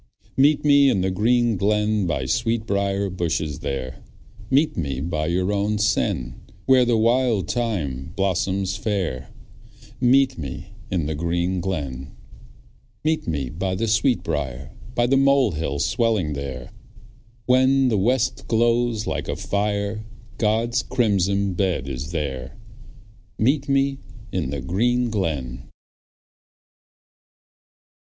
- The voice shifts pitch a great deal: Yes, wide, 7.5 semitones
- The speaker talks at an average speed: No, slow, 120 wpm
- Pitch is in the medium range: No, low, 100 Hz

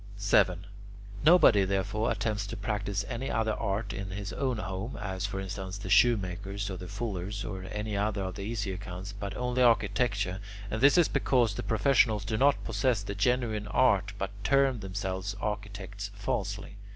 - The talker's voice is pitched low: Yes, low, 100 Hz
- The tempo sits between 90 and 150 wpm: No, average, 170 wpm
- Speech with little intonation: Yes, narrow, 2.3 semitones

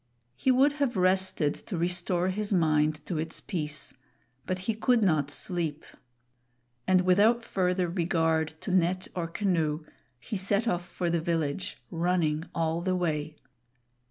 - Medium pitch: Yes, medium, 175 Hz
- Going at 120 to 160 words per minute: Yes, average, 145 wpm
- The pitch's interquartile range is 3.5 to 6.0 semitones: No, average, 2.8 semitones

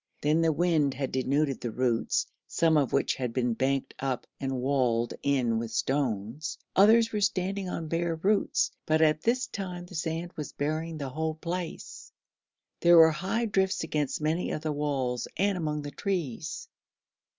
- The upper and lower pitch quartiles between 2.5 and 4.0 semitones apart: No, average, 4.5 semitones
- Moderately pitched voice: Yes, medium, 155 Hz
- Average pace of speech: Yes, average, 170 wpm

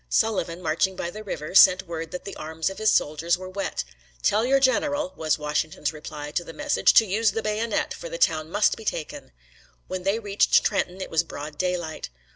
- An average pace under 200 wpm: No, fast, 205 wpm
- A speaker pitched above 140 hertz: Yes, medium, 185 Hz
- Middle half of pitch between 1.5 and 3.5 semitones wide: No, average, 5.2 semitones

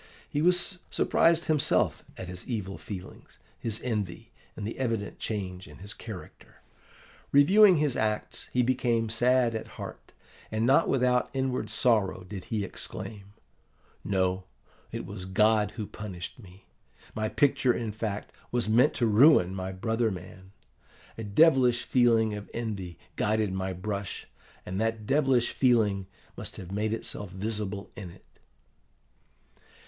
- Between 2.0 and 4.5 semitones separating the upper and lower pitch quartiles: Yes, average, 3.8 semitones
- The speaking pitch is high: No, low, 110 Hz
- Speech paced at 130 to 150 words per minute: Yes, average, 140 wpm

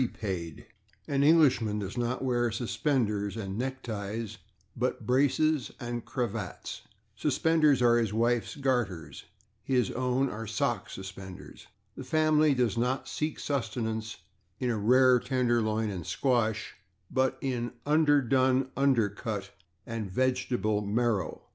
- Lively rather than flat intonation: No, average, 3.4 semitones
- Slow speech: Yes, slow, 120 wpm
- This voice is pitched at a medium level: No, low, 120 Hz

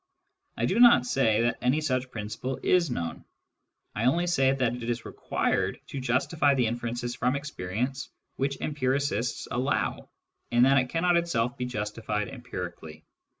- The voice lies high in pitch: No, low, 125 Hz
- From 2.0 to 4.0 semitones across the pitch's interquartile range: Yes, average, 3.0 semitones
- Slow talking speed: No, average, 150 wpm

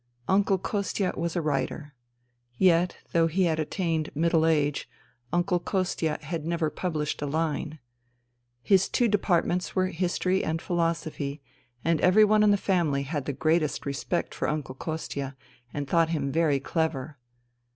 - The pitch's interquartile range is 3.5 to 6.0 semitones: No, average, 3.1 semitones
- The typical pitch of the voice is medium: Yes, medium, 165 Hz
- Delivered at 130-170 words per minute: Yes, average, 150 wpm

